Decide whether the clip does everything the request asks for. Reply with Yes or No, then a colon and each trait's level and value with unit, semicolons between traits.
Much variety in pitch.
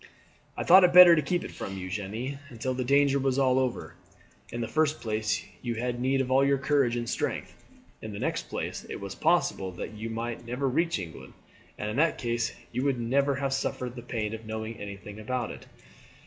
No: average, 3.8 semitones